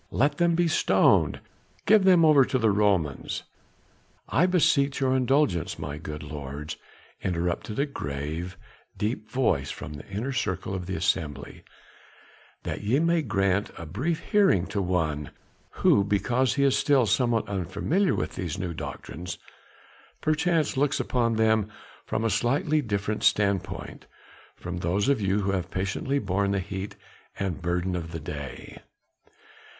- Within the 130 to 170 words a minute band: Yes, average, 145 wpm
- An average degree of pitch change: No, wide, 7.4 semitones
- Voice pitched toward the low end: Yes, low, 100 Hz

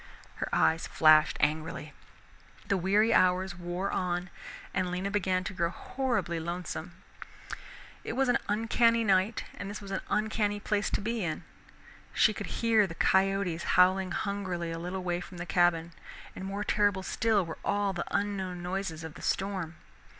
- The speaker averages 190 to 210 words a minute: No, average, 165 wpm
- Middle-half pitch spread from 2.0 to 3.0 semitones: Yes, average, 2.7 semitones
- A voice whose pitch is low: No, high, 190 Hz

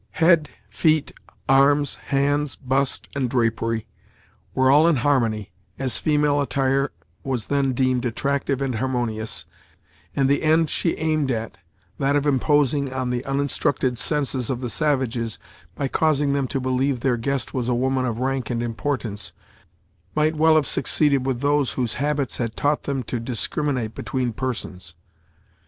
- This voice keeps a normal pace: Yes, average, 150 wpm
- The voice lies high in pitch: No, low, 135 Hz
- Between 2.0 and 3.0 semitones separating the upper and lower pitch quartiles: Yes, average, 2.7 semitones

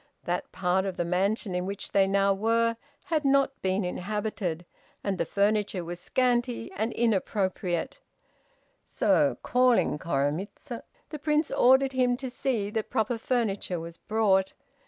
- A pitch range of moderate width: Yes, average, 4.6 semitones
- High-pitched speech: Yes, high, 205 Hz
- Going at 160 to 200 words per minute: No, average, 140 wpm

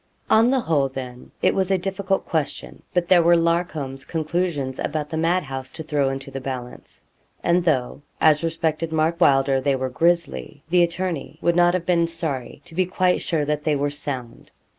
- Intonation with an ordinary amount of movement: Yes, average, 4.1 semitones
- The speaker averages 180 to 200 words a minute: Yes, average, 190 wpm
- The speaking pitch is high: No, medium, 160 Hz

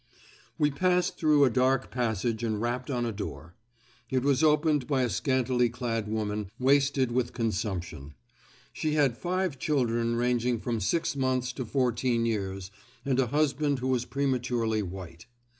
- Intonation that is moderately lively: Yes, average, 3.4 semitones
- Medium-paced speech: Yes, average, 155 wpm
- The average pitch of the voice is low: Yes, low, 125 Hz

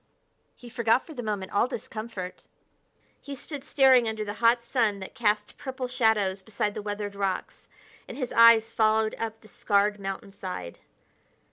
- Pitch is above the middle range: Yes, high, 220 Hz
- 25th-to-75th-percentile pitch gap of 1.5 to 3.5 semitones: Yes, average, 2.8 semitones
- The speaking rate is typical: Yes, average, 155 wpm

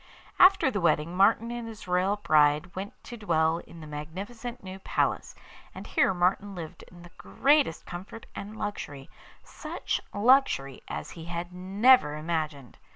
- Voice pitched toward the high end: No, medium, 180 Hz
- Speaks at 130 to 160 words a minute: Yes, average, 155 wpm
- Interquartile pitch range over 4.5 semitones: Yes, average, 4.9 semitones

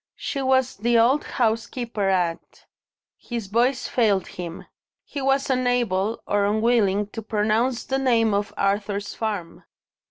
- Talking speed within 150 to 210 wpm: No, slow, 135 wpm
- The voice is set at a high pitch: Yes, high, 225 Hz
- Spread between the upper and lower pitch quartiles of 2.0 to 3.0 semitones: No, average, 3.5 semitones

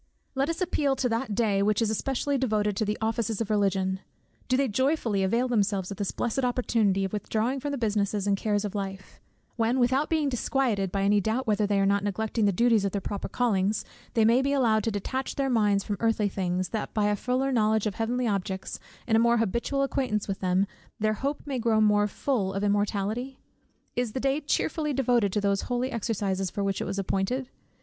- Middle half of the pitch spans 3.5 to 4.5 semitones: Yes, average, 3.8 semitones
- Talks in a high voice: Yes, high, 220 Hz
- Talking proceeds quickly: Yes, fast, 215 wpm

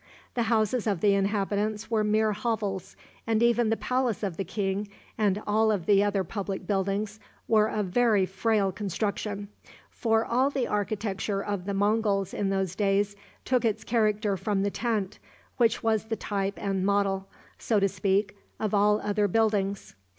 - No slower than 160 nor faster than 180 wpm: Yes, average, 165 wpm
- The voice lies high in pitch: Yes, high, 205 Hz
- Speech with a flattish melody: Yes, narrow, 1.9 semitones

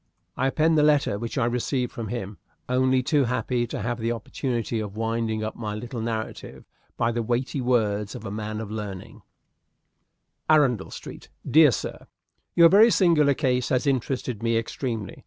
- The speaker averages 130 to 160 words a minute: No, average, 170 wpm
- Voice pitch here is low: Yes, low, 120 Hz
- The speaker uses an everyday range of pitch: Yes, average, 3.1 semitones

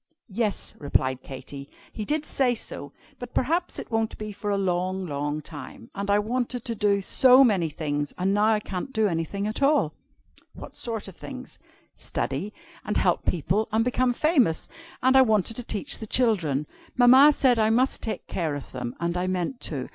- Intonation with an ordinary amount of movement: No, wide, 6.5 semitones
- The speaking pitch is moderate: No, high, 205 Hz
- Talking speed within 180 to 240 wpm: Yes, average, 190 wpm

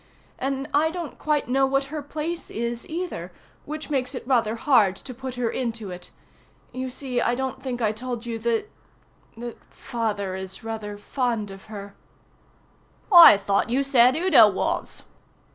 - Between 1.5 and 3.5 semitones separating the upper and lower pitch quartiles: No, average, 3.9 semitones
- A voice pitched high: Yes, high, 245 Hz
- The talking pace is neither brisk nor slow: Yes, average, 160 wpm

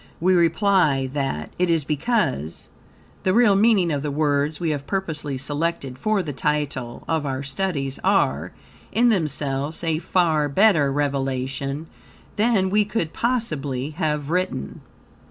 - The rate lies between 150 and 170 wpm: No, slow, 135 wpm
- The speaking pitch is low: No, medium, 150 Hz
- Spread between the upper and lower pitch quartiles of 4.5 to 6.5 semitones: Yes, average, 5.2 semitones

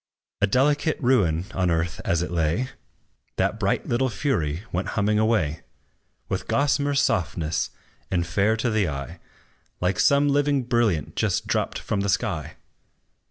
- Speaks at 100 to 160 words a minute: Yes, average, 145 wpm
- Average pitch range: No, wide, 7.4 semitones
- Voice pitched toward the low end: Yes, low, 100 Hz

